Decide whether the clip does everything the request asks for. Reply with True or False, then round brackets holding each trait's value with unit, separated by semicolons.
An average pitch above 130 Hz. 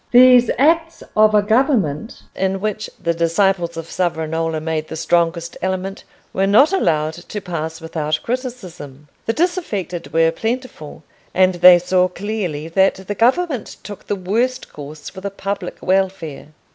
True (185 Hz)